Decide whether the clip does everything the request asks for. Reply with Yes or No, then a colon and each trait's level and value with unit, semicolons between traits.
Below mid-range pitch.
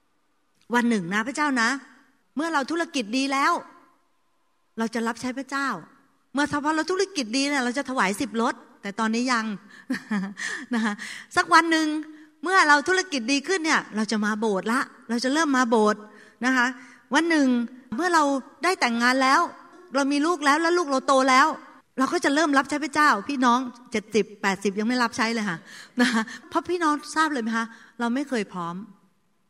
No: very high, 265 Hz